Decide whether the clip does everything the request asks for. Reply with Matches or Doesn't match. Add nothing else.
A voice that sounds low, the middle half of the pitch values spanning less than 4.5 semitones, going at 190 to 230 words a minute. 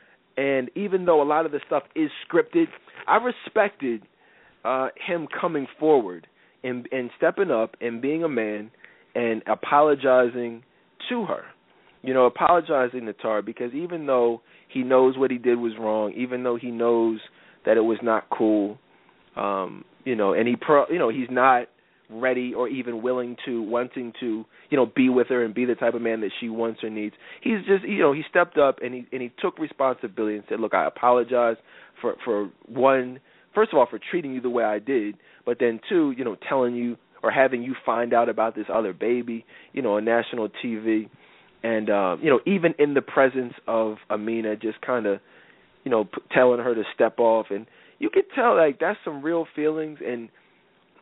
Matches